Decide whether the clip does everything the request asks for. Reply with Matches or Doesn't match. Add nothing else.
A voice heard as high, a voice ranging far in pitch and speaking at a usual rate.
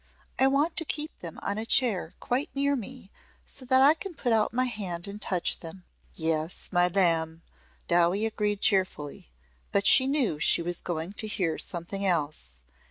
Matches